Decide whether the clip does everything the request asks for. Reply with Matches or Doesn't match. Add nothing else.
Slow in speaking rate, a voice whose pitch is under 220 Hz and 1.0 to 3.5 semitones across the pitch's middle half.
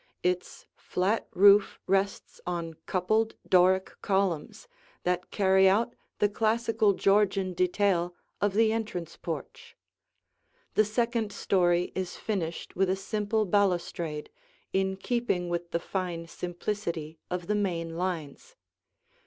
Matches